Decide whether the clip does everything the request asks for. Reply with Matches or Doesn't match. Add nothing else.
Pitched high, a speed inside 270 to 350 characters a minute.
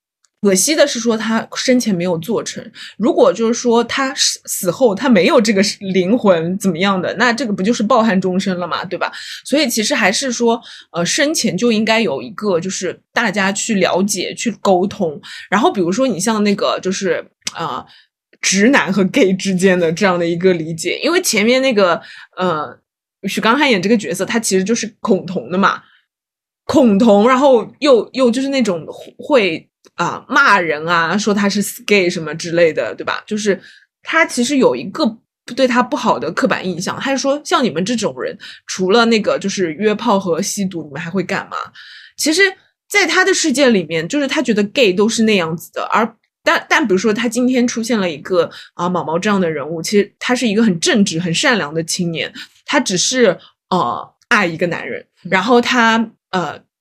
Matches